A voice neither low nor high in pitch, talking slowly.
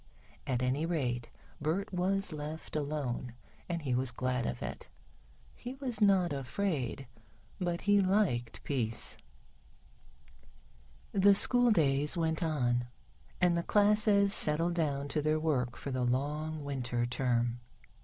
Yes: medium, 150 Hz; slow, 130 wpm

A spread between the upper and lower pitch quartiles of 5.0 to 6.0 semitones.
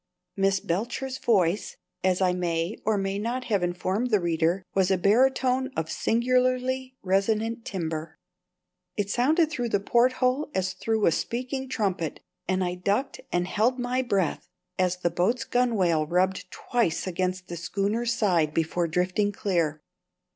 Yes: average, 5.3 semitones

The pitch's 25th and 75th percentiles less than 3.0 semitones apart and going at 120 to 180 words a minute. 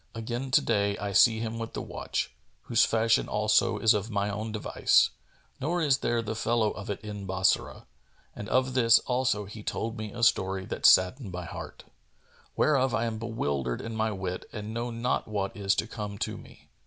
No: narrow, 2.5 semitones; average, 195 wpm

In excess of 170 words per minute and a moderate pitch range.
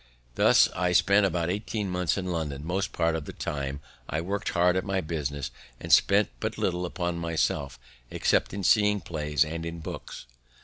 Yes: average, 180 wpm; average, 3.3 semitones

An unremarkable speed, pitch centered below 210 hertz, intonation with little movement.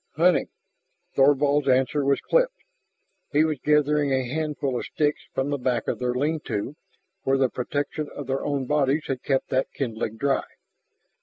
Yes: average, 165 wpm; medium, 140 Hz; narrow, 2.1 semitones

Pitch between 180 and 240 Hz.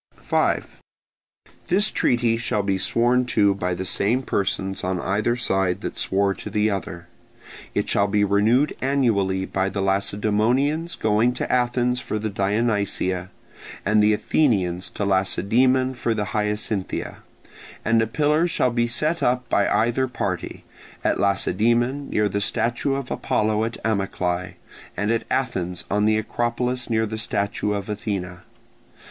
No: low, 110 Hz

